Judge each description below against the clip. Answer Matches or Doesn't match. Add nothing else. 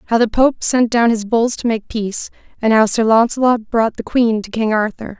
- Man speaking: Doesn't match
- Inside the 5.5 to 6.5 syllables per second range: Doesn't match